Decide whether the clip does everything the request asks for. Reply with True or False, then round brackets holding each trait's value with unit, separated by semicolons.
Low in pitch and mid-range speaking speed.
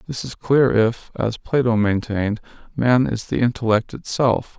True (115 Hz; 155 wpm)